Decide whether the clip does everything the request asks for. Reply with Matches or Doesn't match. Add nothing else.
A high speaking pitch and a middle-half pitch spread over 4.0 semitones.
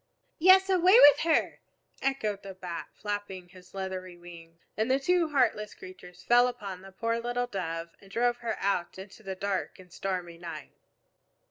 Matches